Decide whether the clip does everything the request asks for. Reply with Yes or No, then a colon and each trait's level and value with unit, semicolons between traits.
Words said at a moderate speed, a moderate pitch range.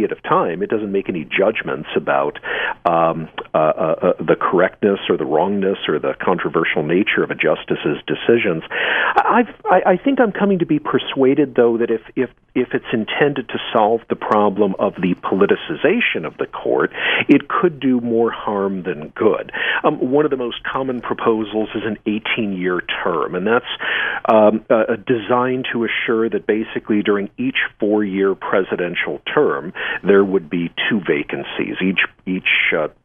Yes: average, 175 wpm; average, 4.2 semitones